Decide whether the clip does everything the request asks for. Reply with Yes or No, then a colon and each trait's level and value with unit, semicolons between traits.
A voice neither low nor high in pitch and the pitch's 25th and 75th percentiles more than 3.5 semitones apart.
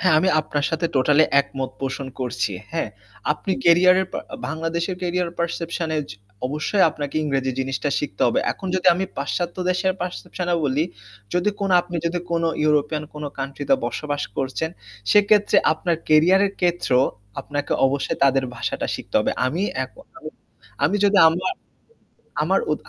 Yes: medium, 160 Hz; average, 4.1 semitones